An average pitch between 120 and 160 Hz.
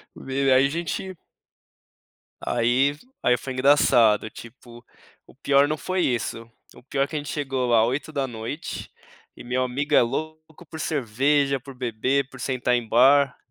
Yes: low, 135 Hz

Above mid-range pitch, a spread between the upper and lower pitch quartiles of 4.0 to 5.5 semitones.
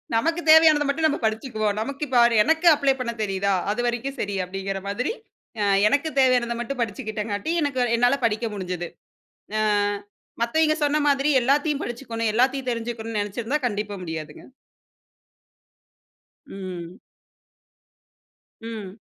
Yes: high, 235 Hz; average, 5.0 semitones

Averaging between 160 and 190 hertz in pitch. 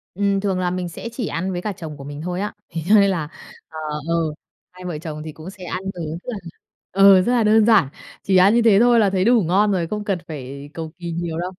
Yes: medium, 185 Hz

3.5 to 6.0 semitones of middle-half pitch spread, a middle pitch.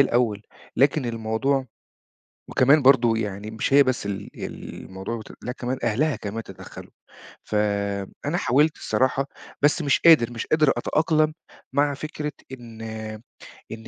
No: average, 4.4 semitones; low, 125 Hz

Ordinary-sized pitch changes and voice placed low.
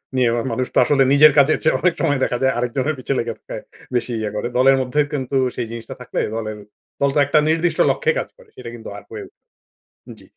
Yes: average, 3.8 semitones; low, 130 Hz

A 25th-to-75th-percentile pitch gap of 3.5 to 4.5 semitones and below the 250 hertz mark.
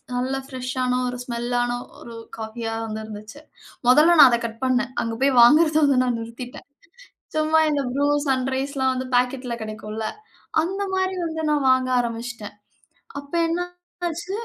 No: average, 3.9 semitones; very high, 255 Hz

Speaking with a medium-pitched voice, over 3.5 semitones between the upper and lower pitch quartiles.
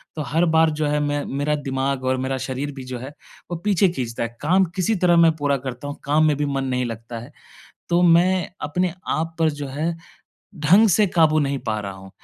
Yes: medium, 145 Hz; average, 4.1 semitones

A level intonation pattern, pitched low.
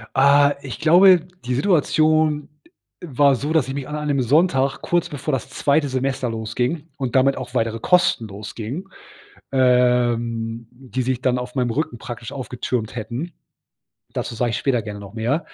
No: average, 3.5 semitones; low, 130 Hz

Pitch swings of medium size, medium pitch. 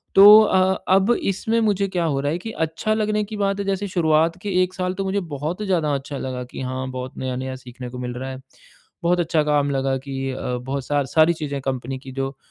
No: wide, 6.2 semitones; medium, 155 Hz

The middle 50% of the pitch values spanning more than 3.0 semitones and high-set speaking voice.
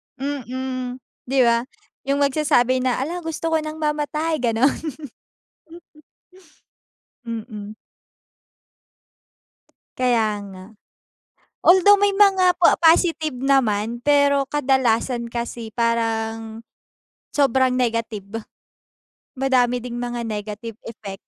Yes: average, 4.0 semitones; very high, 250 Hz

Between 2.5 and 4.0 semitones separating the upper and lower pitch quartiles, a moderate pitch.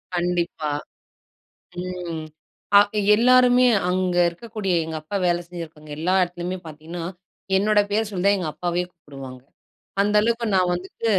Yes: average, 3.4 semitones; medium, 180 Hz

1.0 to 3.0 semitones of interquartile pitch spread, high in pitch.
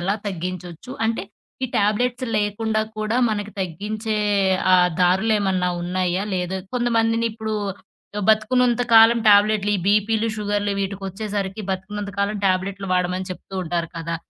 Yes: average, 2.7 semitones; high, 205 Hz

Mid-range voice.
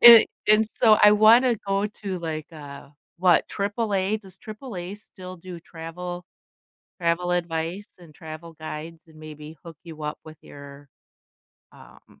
Yes: medium, 175 Hz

